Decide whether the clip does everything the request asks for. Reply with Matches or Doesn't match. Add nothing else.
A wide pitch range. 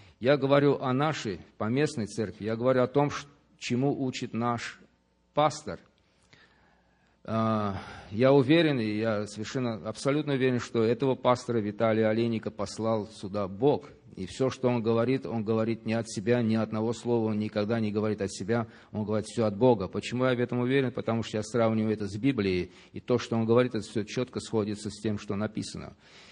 Doesn't match